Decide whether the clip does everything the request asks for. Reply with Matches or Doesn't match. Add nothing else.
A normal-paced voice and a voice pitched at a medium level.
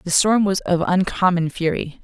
Matches